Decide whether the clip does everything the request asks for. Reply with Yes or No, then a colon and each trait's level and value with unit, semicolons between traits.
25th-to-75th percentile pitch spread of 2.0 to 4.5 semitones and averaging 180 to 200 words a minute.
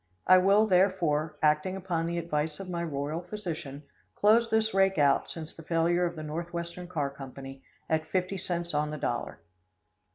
No: average, 3.4 semitones; average, 170 wpm